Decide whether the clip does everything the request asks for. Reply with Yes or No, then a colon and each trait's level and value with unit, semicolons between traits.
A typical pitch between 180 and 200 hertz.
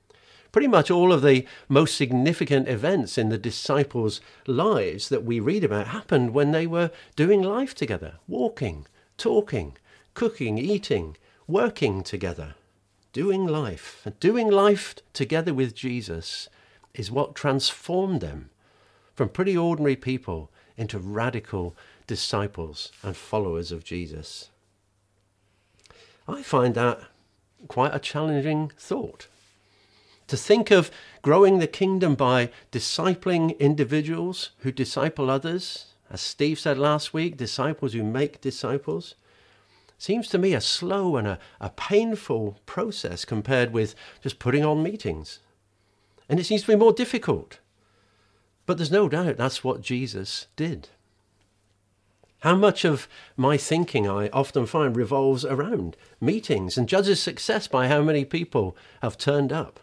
No: low, 135 Hz